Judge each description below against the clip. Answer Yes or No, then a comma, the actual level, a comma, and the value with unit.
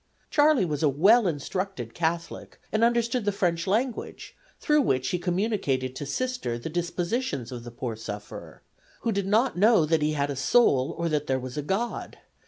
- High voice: No, medium, 170 Hz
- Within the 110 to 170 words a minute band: No, average, 185 wpm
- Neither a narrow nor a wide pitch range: No, wide, 8.1 semitones